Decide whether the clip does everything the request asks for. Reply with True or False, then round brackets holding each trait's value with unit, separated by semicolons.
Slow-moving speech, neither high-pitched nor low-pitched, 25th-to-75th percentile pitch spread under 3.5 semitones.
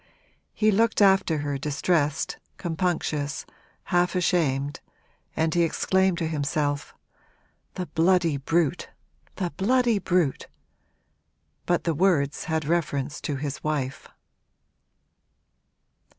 False (100 wpm; 165 Hz; 3.9 semitones)